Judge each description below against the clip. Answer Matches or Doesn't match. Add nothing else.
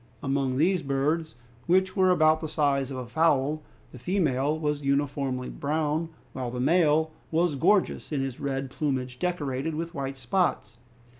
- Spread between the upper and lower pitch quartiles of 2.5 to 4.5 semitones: Matches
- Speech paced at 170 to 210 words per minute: Doesn't match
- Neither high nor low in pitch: Matches